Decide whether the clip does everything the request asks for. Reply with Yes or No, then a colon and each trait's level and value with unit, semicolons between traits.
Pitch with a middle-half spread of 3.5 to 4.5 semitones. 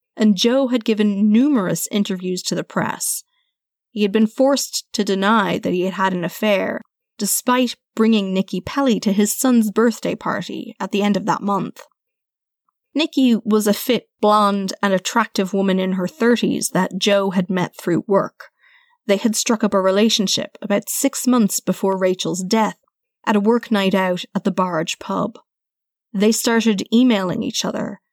Yes: average, 3.9 semitones